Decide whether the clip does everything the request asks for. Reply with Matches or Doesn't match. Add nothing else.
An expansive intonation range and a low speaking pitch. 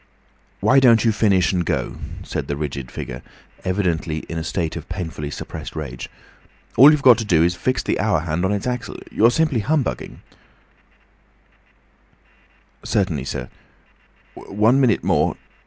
Matches